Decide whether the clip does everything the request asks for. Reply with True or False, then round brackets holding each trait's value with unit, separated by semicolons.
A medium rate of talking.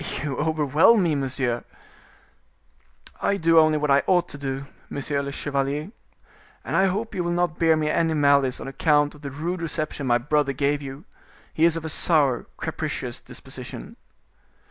True (170 wpm)